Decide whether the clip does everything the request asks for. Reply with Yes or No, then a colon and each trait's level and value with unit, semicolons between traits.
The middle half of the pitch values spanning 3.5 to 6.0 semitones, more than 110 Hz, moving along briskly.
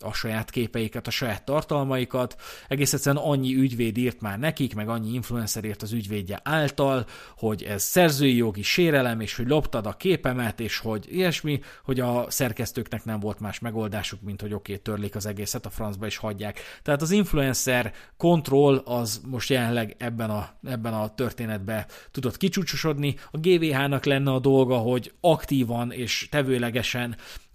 Yes: average, 4.0 semitones; low, 120 Hz; fast, 160 wpm